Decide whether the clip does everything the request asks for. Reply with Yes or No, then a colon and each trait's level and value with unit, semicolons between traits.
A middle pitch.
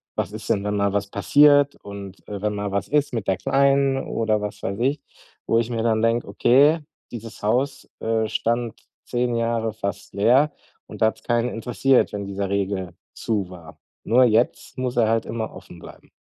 No: low, 115 Hz